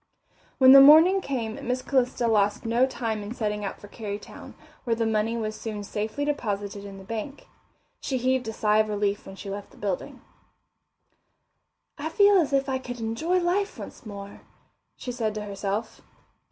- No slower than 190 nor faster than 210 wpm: No, average, 180 wpm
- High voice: Yes, high, 225 Hz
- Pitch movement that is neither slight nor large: Yes, average, 4.1 semitones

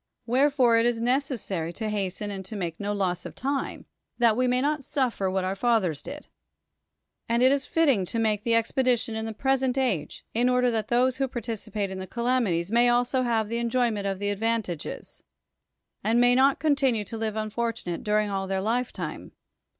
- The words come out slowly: No, average, 195 wpm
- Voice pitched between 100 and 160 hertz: No, high, 230 Hz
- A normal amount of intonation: Yes, average, 3.6 semitones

